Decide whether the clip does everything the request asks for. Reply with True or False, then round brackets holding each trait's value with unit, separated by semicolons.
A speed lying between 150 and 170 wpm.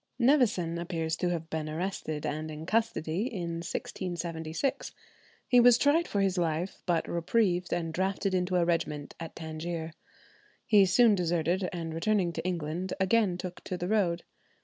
True (155 wpm)